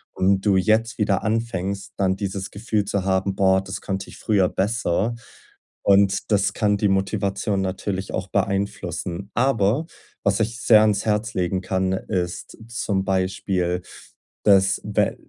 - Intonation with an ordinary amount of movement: No, narrow, 1.8 semitones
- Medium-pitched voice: No, low, 100 Hz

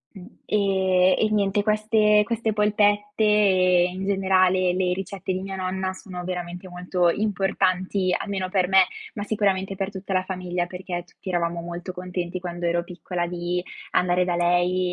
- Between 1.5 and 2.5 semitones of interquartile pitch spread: Yes, narrow, 1.9 semitones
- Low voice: No, medium, 185 Hz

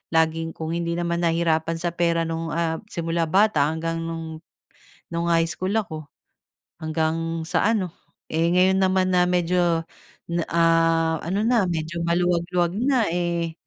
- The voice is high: No, medium, 170 Hz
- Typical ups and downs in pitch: No, narrow, 1.4 semitones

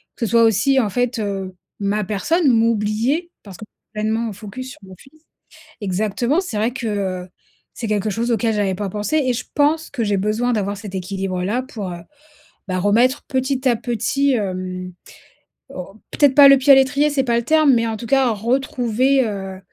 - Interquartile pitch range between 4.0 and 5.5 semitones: Yes, average, 4.5 semitones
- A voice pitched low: No, high, 225 Hz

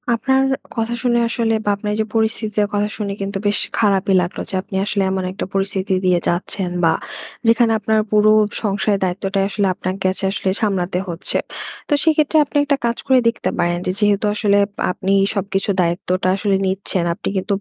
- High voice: Yes, high, 200 Hz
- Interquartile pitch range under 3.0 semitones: Yes, narrow, 2.5 semitones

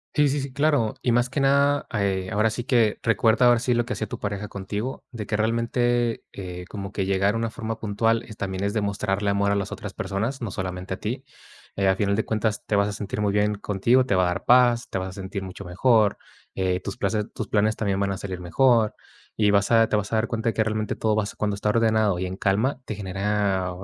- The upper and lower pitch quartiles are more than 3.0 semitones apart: No, average, 2.7 semitones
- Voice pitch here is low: Yes, low, 105 Hz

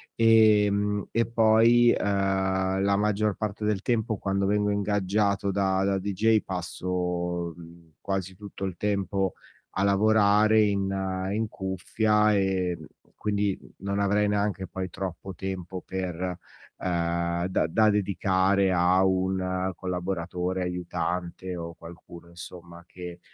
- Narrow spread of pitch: Yes, narrow, 2.2 semitones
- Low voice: Yes, very low, 95 Hz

